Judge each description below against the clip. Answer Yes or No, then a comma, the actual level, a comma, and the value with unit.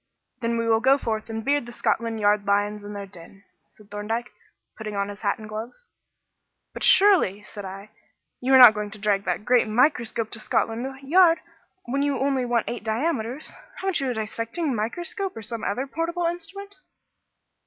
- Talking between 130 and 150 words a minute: No, average, 185 wpm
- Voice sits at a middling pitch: No, high, 230 Hz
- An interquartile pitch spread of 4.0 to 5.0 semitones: Yes, average, 4.6 semitones